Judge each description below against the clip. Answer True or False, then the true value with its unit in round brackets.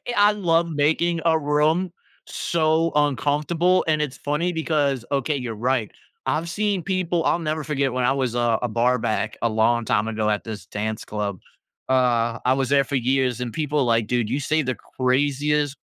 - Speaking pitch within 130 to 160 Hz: True (140 Hz)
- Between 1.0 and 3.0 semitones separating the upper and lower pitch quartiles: False (4.8 semitones)